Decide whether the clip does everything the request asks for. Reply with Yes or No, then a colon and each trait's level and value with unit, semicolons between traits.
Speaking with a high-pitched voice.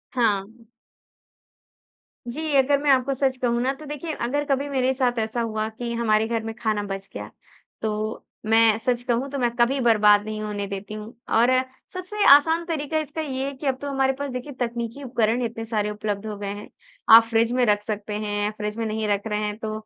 Yes: high, 230 Hz